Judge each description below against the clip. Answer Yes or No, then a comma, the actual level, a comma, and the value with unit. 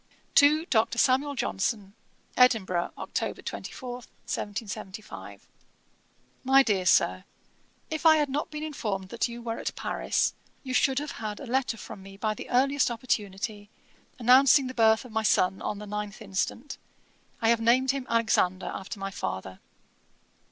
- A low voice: No, high, 230 Hz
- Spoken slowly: No, average, 150 wpm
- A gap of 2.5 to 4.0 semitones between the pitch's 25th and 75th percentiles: No, average, 4.4 semitones